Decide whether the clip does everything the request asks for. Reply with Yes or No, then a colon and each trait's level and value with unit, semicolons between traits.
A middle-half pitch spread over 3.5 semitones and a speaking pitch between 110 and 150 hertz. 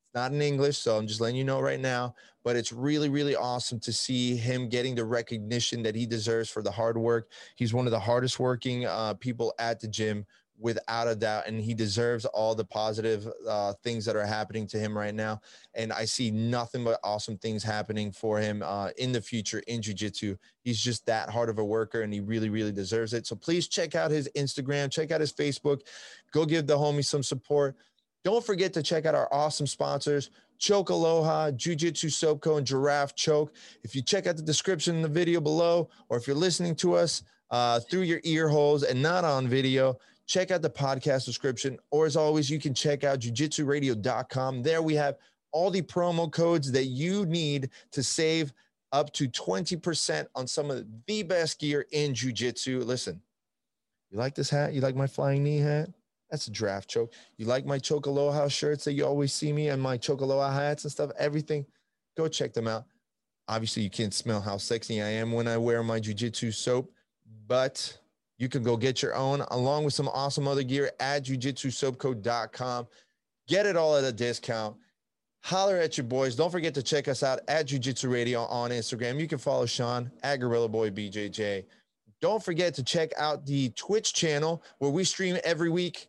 Yes: average, 4.4 semitones; low, 135 Hz